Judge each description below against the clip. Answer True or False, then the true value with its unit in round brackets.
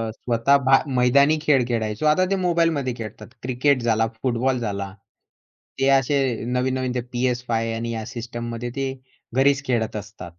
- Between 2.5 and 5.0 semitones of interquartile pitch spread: True (2.8 semitones)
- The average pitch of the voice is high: False (125 Hz)